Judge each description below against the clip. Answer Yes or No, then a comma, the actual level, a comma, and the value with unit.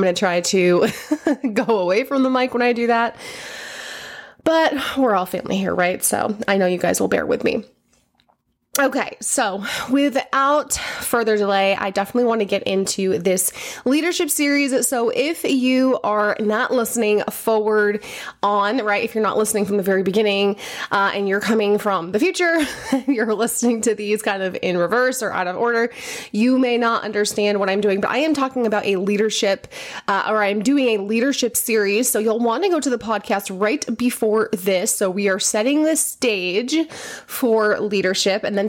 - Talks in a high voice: Yes, high, 220 Hz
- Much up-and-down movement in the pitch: No, average, 4.2 semitones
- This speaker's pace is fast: No, average, 185 wpm